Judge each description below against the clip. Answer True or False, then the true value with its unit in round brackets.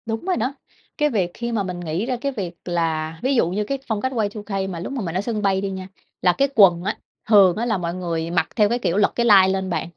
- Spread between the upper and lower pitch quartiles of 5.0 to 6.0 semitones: False (4.6 semitones)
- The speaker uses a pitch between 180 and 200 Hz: True (195 Hz)